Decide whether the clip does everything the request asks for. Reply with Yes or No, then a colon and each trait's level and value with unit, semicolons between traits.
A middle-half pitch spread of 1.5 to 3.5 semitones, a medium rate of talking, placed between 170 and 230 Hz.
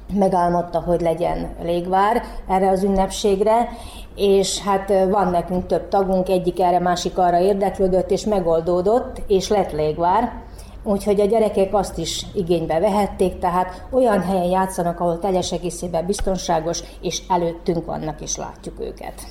Yes: narrow, 2.4 semitones; average, 135 wpm; high, 190 Hz